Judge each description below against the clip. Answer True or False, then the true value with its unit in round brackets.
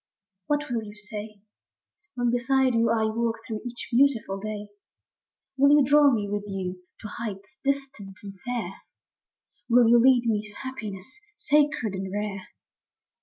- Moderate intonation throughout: True (4.1 semitones)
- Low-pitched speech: False (230 Hz)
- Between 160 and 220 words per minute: False (150 wpm)